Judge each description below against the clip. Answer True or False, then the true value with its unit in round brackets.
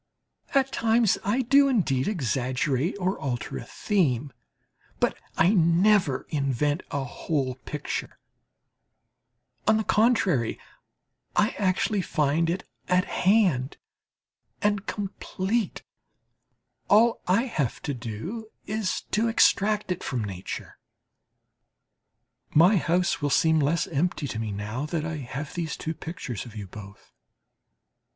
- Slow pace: True (120 wpm)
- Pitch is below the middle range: False (165 Hz)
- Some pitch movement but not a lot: False (7.5 semitones)